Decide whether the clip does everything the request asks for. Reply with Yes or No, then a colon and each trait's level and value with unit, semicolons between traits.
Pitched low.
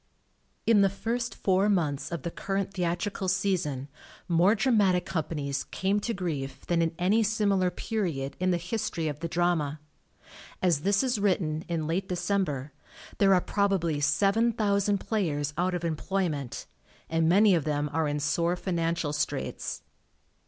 No: medium, 175 Hz